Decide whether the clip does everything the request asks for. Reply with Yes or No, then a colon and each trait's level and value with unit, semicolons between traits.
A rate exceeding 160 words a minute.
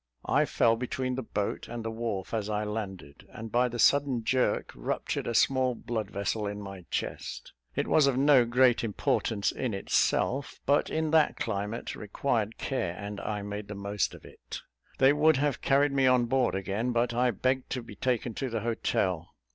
Yes: average, 185 wpm